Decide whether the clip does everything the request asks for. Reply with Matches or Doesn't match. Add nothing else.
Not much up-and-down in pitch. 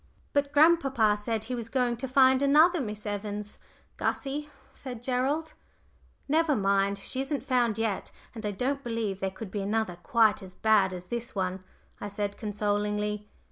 Doesn't match